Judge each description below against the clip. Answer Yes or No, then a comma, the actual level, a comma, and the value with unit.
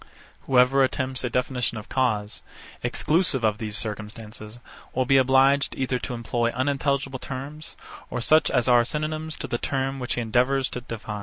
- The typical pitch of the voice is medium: No, low, 130 Hz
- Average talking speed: Yes, average, 165 wpm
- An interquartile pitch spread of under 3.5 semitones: Yes, narrow, 2.6 semitones